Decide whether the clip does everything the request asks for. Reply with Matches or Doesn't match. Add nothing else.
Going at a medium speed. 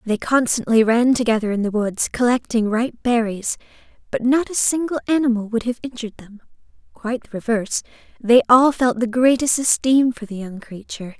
Matches